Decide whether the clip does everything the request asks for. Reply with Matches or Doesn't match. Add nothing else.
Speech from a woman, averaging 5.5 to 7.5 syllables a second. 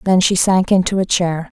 Doesn't match